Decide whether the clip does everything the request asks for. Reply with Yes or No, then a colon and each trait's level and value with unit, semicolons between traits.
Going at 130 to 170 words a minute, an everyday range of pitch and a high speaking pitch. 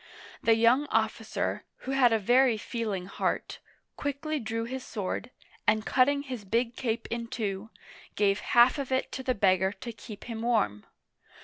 Yes: average, 165 wpm; average, 3.5 semitones; high, 230 Hz